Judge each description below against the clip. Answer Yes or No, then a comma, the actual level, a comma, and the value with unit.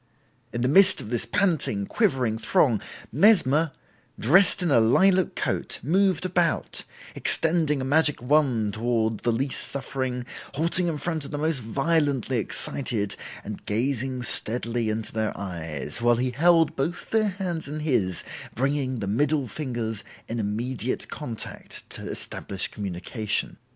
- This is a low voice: Yes, low, 130 Hz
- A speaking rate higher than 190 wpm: No, average, 140 wpm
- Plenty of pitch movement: Yes, wide, 6.1 semitones